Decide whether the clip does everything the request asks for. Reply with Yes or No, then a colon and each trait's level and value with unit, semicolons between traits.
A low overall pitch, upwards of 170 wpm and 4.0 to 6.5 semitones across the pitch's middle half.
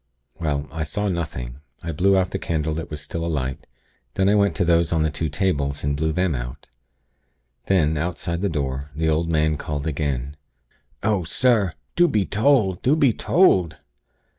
Yes: very low, 80 Hz; average, 185 wpm; average, 4.5 semitones